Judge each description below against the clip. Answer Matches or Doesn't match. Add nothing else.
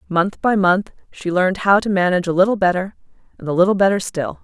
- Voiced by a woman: Matches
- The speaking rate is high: Matches